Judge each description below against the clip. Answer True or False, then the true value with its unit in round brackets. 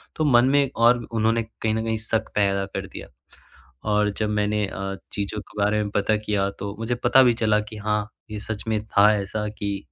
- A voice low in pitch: True (105 Hz)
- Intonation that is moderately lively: False (1.5 semitones)